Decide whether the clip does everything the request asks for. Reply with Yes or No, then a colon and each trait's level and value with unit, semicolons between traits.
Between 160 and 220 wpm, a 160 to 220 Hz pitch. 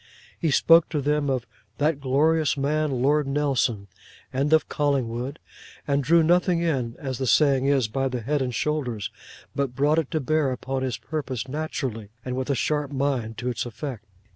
No: average, 180 wpm; medium, 140 Hz